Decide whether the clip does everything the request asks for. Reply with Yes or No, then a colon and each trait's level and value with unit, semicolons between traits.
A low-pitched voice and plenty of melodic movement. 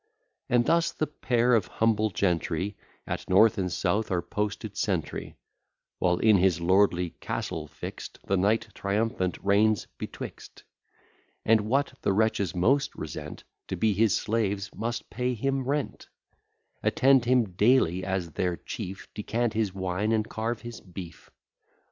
No: low, 105 Hz; average, 3.7 semitones